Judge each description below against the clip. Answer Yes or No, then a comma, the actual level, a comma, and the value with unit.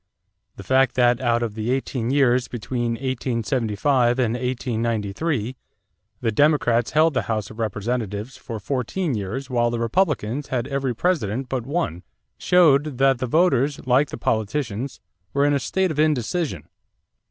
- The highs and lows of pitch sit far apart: No, average, 3.4 semitones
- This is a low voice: Yes, low, 125 Hz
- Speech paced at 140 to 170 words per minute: Yes, average, 150 wpm